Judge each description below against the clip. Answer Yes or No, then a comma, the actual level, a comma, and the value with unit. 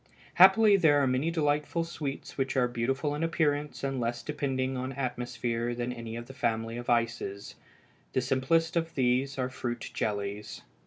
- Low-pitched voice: Yes, low, 130 Hz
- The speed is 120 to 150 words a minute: No, average, 165 wpm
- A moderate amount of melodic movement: Yes, average, 3.6 semitones